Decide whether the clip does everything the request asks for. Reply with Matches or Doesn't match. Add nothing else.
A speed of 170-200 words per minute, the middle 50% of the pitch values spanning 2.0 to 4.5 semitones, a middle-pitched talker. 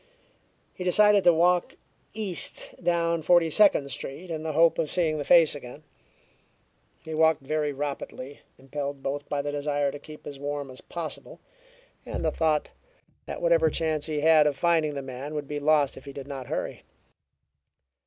Matches